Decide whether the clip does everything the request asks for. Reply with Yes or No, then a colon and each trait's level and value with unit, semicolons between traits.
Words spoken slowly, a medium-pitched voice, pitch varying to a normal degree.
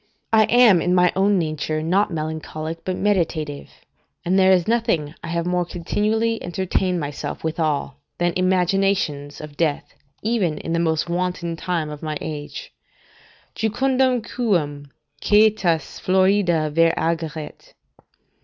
Yes: slow, 130 wpm; medium, 175 Hz; average, 3.8 semitones